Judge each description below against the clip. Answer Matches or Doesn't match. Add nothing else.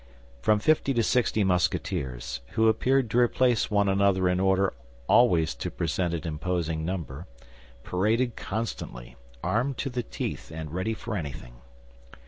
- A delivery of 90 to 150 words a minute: Matches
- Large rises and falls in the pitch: Matches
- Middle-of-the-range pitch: Doesn't match